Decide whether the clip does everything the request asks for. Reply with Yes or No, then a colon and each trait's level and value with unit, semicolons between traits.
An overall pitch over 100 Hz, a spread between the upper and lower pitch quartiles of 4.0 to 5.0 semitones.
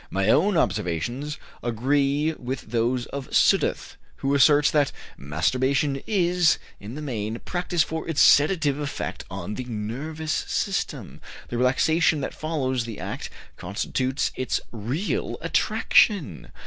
Yes: low, 135 Hz; average, 4.6 semitones